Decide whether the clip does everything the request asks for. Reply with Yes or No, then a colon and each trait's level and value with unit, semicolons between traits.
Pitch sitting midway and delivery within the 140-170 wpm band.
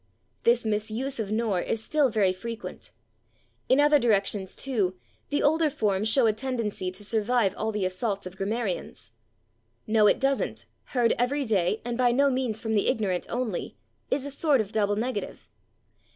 No: high, 220 Hz; average, 165 wpm